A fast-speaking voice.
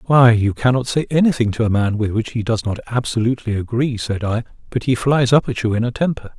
Yes: fast, 245 wpm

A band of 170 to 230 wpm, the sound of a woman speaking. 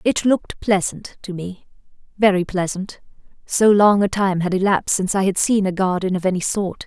Yes: average, 185 wpm; female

